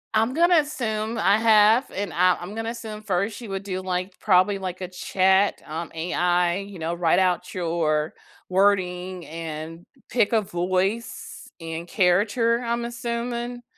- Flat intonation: No, average, 4.0 semitones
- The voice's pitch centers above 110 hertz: Yes, high, 190 Hz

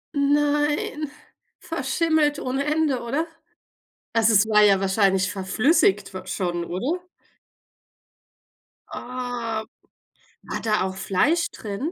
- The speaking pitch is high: Yes, high, 230 Hz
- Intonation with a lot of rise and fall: Yes, wide, 7.1 semitones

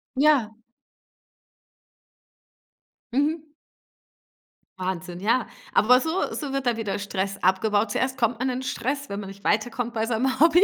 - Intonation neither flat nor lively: Yes, average, 4.9 semitones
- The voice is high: Yes, high, 235 Hz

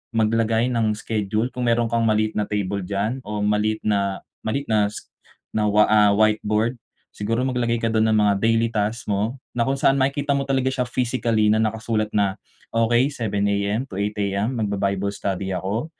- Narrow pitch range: Yes, narrow, 2.2 semitones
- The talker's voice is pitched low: Yes, low, 110 Hz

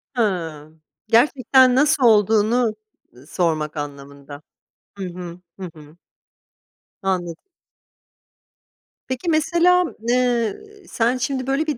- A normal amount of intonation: No, wide, 7.6 semitones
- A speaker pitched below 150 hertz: No, high, 220 Hz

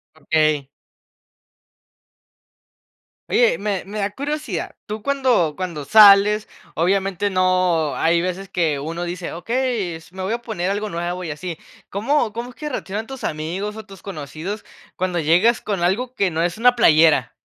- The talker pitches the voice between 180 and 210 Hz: Yes, high, 190 Hz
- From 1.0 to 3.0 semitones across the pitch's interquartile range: No, average, 4.3 semitones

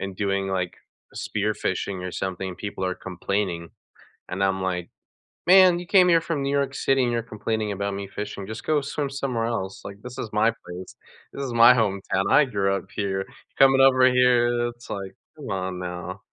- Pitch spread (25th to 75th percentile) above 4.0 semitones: Yes, average, 5.0 semitones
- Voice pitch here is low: Yes, low, 105 Hz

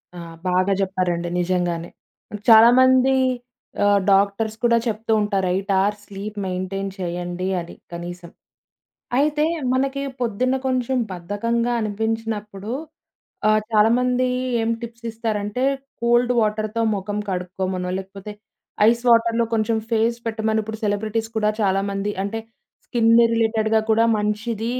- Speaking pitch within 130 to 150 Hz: No, high, 215 Hz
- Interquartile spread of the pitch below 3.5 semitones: Yes, average, 2.9 semitones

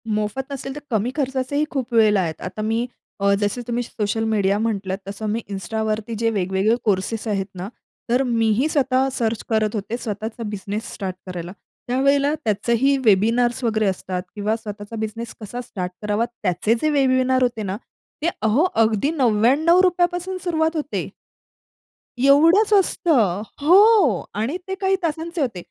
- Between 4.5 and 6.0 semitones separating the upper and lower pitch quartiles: Yes, average, 4.9 semitones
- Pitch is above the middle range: Yes, high, 230 Hz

